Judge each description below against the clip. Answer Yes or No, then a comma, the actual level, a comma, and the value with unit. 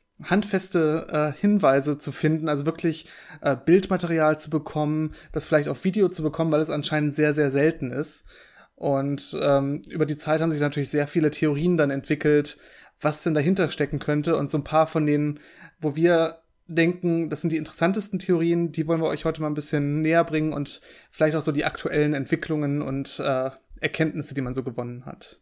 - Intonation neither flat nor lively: No, narrow, 1.8 semitones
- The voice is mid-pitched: Yes, medium, 155 Hz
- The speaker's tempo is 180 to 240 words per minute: Yes, fast, 190 wpm